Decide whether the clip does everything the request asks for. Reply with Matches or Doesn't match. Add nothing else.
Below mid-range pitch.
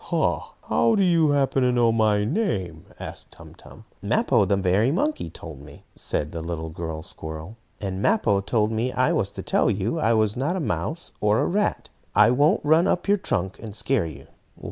Matches